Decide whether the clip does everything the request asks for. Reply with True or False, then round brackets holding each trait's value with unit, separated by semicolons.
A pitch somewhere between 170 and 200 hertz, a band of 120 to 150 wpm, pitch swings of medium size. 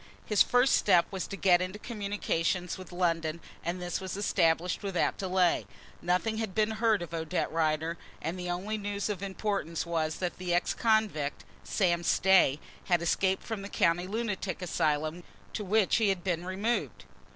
False (185 Hz; 170 wpm; 3.0 semitones)